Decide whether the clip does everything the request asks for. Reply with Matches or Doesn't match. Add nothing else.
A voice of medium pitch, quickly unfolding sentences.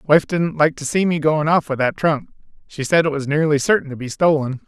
Matches